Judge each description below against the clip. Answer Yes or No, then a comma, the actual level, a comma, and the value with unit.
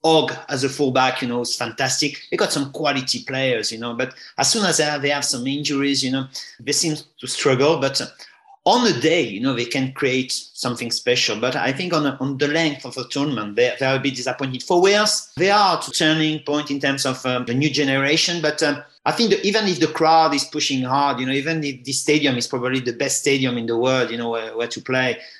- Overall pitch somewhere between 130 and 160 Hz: Yes, medium, 140 Hz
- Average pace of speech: No, fast, 245 wpm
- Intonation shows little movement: No, average, 3.1 semitones